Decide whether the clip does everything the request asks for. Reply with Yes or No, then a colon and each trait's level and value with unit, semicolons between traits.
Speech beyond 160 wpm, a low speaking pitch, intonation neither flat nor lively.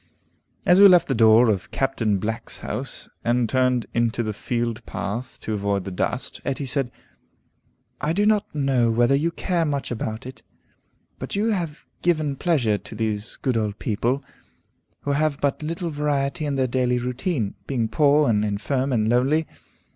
Yes: average, 170 wpm; low, 130 Hz; average, 4.8 semitones